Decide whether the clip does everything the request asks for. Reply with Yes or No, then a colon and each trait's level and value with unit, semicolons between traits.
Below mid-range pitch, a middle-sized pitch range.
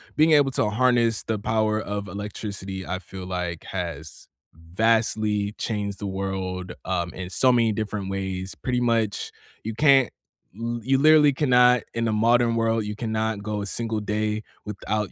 Yes: low, 110 Hz; average, 3.1 semitones